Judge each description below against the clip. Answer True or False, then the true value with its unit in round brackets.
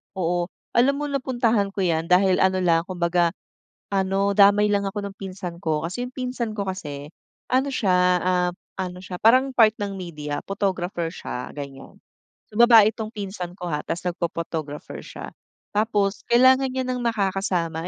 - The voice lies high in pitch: True (195 Hz)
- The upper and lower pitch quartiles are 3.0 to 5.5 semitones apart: True (4.1 semitones)